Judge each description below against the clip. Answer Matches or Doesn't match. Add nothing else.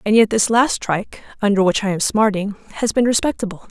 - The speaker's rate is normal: Doesn't match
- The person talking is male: Doesn't match